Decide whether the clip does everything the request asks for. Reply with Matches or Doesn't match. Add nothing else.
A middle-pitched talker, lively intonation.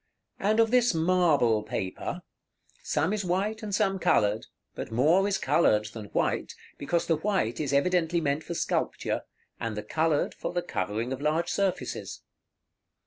Matches